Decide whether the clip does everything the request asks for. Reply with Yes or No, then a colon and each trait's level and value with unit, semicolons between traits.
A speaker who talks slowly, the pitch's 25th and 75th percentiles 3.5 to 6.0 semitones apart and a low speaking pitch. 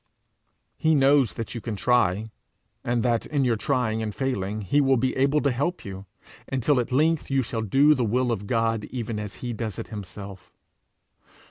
No: average, 190 wpm; average, 3.9 semitones; low, 120 Hz